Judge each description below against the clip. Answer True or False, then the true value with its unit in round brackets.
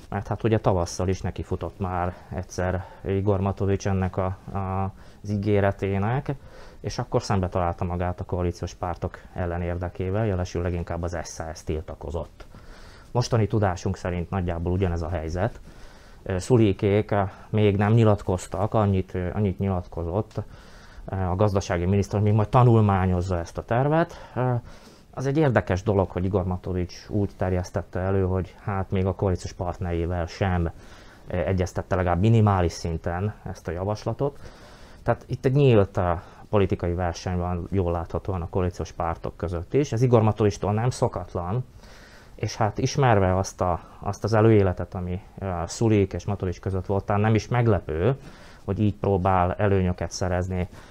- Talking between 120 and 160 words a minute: True (140 wpm)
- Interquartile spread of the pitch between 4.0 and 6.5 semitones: False (2.9 semitones)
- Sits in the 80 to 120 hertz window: True (95 Hz)